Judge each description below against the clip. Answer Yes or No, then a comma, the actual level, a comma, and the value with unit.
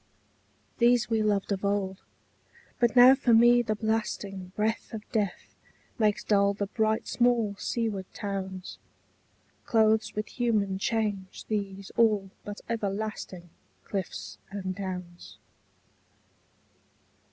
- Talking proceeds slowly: Yes, slow, 110 wpm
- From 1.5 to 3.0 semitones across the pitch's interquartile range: Yes, narrow, 2.4 semitones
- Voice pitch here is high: Yes, high, 210 Hz